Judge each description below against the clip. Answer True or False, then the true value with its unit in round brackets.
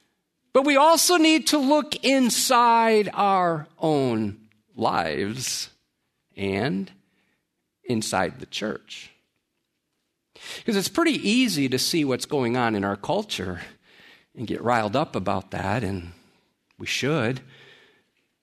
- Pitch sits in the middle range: True (150 Hz)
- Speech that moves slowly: True (115 wpm)